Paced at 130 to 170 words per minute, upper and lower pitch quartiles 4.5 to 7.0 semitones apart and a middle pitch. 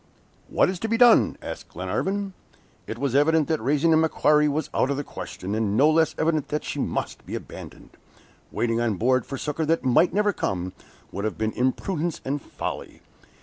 No: average, 190 wpm; average, 5.2 semitones; medium, 145 Hz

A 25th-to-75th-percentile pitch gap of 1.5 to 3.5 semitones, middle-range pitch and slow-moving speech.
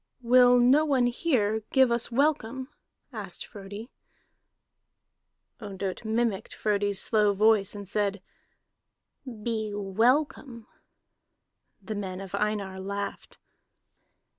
No: average, 3.2 semitones; high, 215 Hz; slow, 95 wpm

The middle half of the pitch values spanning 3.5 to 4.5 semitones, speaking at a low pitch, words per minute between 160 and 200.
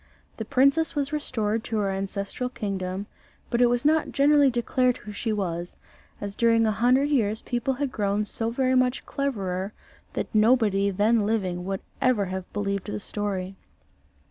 No: average, 4.2 semitones; high, 220 Hz; average, 165 wpm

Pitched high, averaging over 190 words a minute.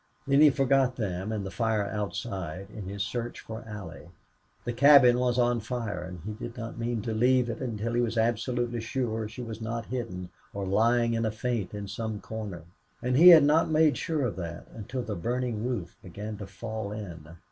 No: low, 115 Hz; average, 200 wpm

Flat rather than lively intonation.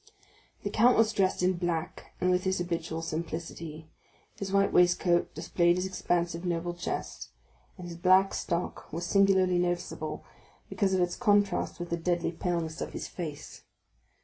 Yes: narrow, 1.8 semitones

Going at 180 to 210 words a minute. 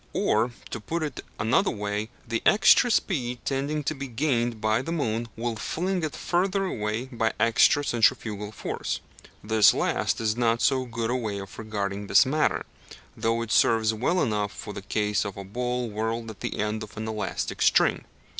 Yes: average, 185 wpm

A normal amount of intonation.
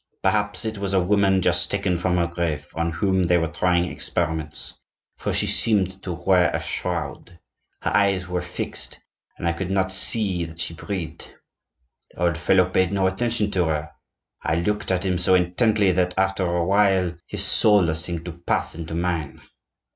No: narrow, 2.1 semitones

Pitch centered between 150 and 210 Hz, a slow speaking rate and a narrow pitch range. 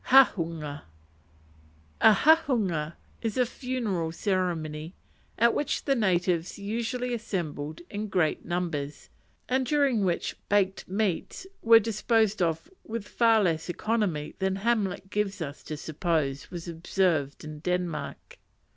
No: high, 190 Hz; slow, 120 wpm; wide, 5.6 semitones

